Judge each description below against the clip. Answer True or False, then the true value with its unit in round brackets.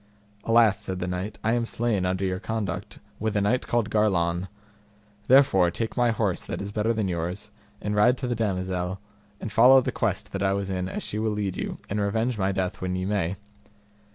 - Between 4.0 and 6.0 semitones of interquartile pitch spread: False (3.3 semitones)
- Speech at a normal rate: False (210 wpm)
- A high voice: False (100 Hz)